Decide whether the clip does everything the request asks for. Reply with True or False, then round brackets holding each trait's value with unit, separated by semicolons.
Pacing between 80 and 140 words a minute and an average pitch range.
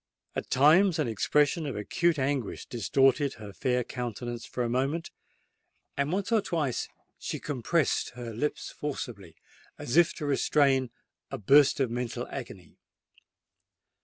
True (135 wpm; 3.7 semitones)